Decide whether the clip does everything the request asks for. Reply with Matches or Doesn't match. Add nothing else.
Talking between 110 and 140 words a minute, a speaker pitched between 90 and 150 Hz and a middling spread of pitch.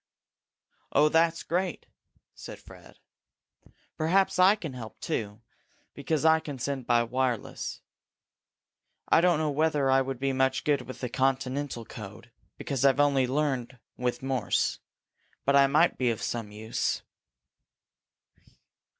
Matches